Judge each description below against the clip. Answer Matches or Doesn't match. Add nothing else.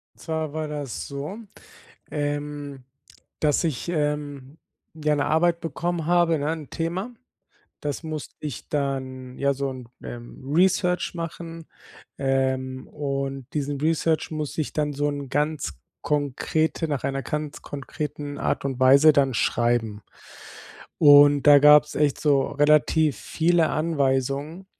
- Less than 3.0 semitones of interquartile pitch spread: Matches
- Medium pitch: Matches